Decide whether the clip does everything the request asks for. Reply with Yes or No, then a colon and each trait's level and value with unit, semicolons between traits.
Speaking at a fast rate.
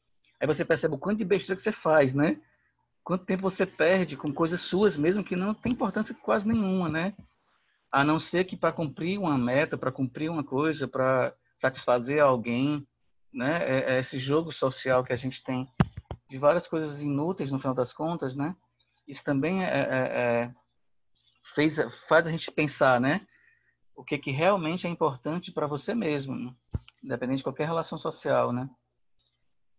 No: average, 175 wpm